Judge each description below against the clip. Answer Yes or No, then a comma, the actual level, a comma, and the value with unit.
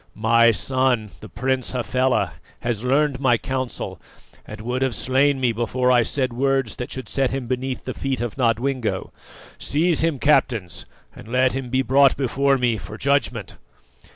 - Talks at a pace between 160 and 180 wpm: Yes, average, 165 wpm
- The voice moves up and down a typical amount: No, narrow, 2.3 semitones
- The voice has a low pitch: Yes, low, 130 Hz